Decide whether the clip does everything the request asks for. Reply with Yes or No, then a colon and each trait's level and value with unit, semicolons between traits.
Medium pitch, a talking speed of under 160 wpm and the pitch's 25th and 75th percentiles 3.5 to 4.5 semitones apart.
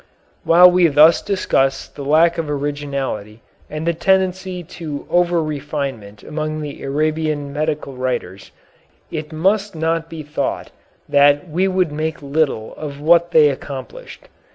No: medium, 155 Hz; slow, 135 wpm; average, 3.0 semitones